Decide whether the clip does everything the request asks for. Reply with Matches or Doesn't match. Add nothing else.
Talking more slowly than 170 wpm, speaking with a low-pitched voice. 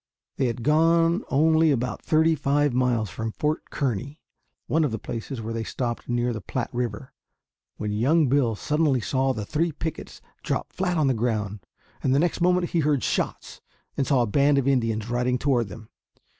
Doesn't match